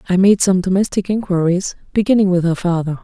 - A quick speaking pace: No, average, 180 wpm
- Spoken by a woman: Yes, female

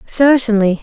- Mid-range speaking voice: No, high, 230 Hz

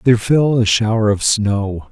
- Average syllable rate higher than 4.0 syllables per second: Yes, 4.5 syllables/s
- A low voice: Yes, low, 110 Hz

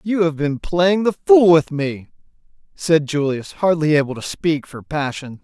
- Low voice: No, medium, 155 Hz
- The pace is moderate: Yes, average, 175 wpm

